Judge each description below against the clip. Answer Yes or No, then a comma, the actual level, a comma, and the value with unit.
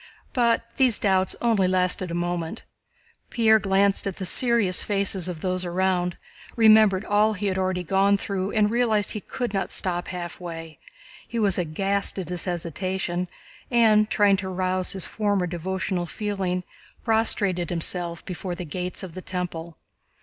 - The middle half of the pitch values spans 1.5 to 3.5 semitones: Yes, narrow, 2.5 semitones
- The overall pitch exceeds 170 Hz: Yes, high, 190 Hz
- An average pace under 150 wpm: No, average, 155 wpm